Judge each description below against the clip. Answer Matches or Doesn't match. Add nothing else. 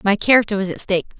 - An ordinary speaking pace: Doesn't match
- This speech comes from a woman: Matches